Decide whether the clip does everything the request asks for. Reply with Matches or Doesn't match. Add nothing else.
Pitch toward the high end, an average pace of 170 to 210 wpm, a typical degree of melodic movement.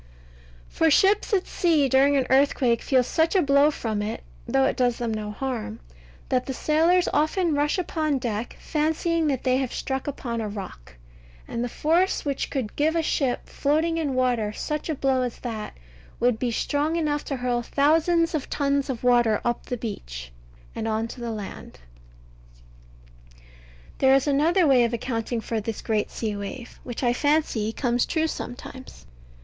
Matches